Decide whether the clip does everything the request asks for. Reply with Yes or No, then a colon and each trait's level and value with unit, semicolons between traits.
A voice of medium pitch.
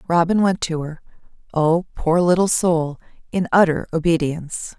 Yes: medium, 170 Hz